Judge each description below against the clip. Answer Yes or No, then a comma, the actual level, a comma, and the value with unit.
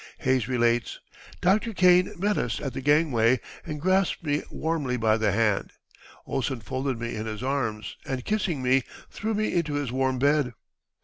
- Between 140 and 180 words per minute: Yes, average, 170 wpm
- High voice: No, low, 130 Hz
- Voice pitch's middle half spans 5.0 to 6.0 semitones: Yes, average, 5.3 semitones